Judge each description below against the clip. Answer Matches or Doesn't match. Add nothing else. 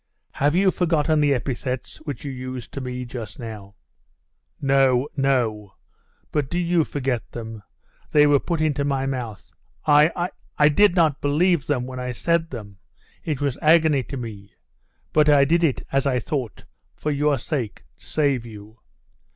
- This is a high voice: Doesn't match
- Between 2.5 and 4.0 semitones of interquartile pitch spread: Matches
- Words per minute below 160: Doesn't match